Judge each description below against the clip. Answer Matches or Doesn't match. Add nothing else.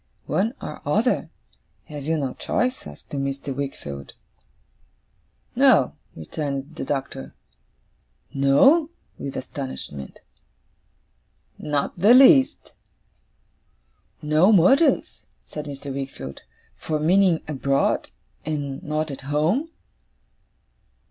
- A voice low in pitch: Doesn't match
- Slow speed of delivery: Matches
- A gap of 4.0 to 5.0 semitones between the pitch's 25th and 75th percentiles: Matches